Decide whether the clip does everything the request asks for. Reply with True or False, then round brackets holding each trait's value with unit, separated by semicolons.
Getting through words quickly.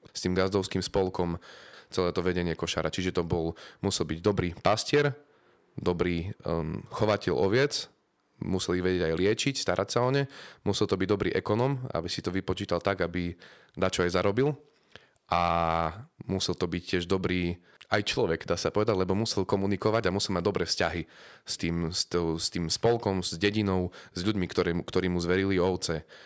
True (170 wpm)